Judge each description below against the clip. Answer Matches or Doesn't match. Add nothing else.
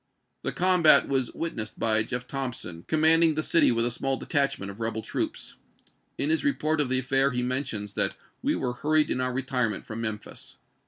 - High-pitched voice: Doesn't match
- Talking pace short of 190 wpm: Doesn't match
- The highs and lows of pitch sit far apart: Doesn't match